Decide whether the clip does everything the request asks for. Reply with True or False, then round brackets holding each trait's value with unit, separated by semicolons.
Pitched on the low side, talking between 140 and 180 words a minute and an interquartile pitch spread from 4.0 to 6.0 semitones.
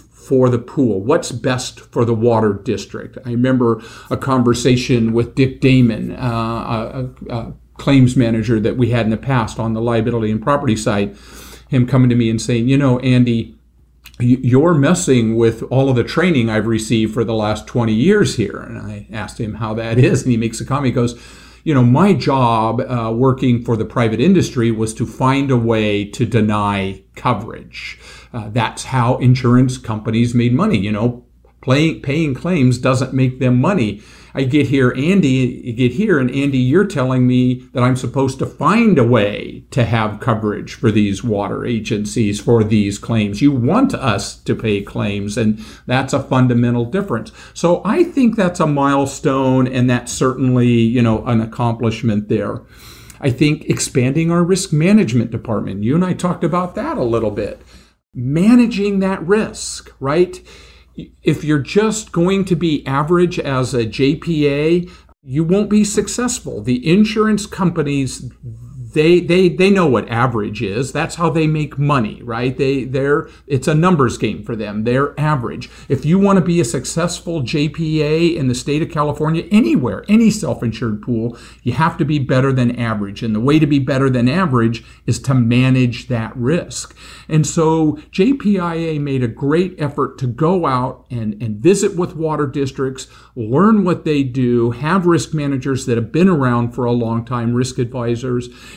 True (130 Hz; 175 wpm; 4.7 semitones)